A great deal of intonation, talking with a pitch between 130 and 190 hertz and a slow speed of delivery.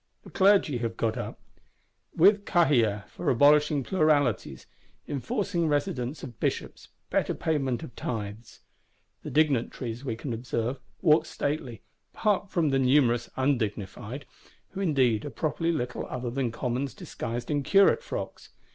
No: average, 4.6 semitones; low, 135 Hz; slow, 130 wpm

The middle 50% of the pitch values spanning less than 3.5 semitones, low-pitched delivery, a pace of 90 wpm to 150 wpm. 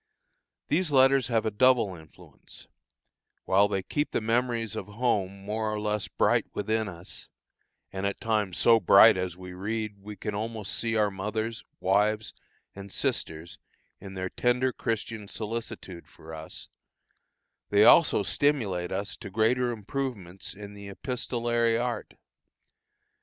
Yes: average, 2.9 semitones; low, 105 Hz; average, 140 wpm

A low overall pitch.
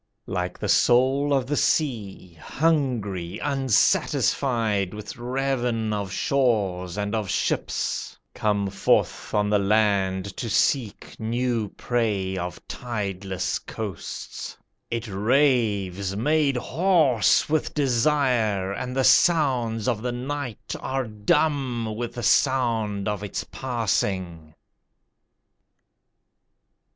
Yes: low, 115 Hz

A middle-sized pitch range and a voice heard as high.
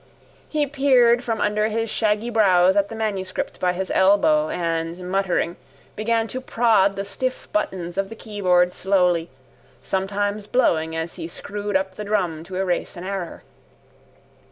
Yes: average, 3.1 semitones; high, 195 Hz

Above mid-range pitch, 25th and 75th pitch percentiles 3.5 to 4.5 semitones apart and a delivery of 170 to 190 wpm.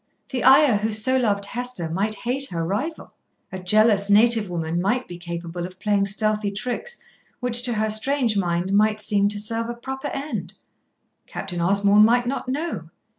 Yes: high, 215 Hz; average, 4.0 semitones; average, 175 wpm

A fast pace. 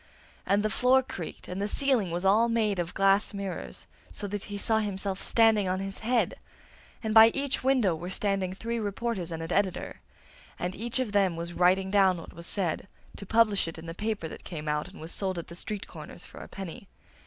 Yes: fast, 215 wpm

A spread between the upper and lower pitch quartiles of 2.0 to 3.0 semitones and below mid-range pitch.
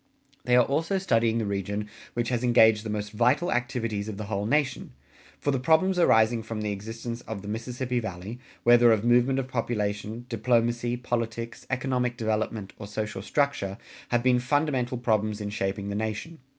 Yes: average, 2.7 semitones; low, 115 Hz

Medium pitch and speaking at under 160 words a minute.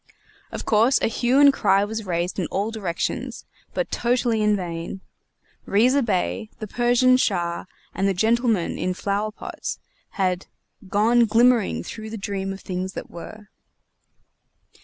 No: high, 210 Hz; average, 145 wpm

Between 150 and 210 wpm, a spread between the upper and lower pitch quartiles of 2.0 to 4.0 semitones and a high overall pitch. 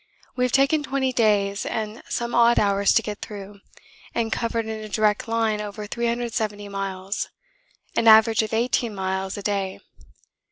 Yes: average, 160 wpm; narrow, 2.5 semitones; high, 215 Hz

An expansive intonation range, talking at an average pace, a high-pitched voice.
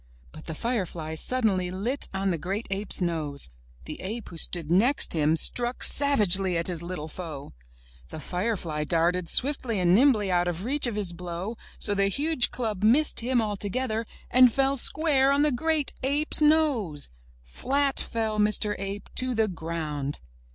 Yes: wide, 6.7 semitones; average, 165 wpm; high, 205 Hz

